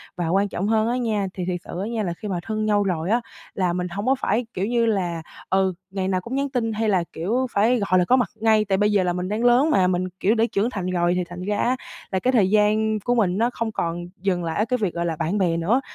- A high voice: Yes, high, 200 Hz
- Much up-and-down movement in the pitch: No, average, 3.7 semitones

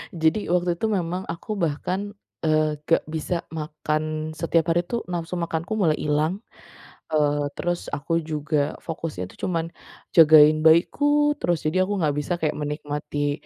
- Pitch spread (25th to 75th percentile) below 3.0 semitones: Yes, narrow, 2.4 semitones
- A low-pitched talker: No, medium, 160 Hz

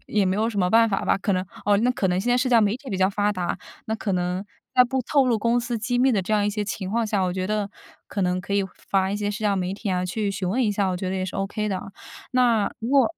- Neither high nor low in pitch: No, high, 205 Hz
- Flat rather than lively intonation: No, average, 3.3 semitones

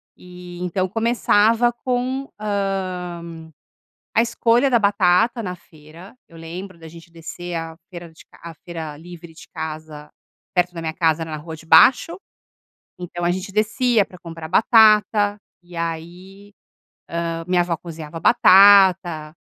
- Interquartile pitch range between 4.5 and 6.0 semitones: No, average, 3.7 semitones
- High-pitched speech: No, medium, 180 Hz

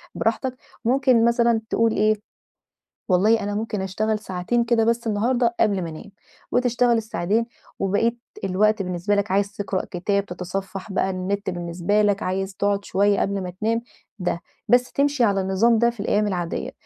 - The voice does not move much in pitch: No, average, 3.2 semitones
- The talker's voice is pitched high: Yes, high, 205 Hz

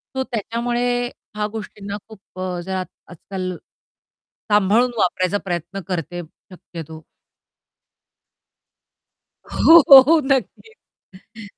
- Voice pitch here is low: No, high, 200 Hz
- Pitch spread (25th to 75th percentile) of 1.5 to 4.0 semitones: No, average, 4.4 semitones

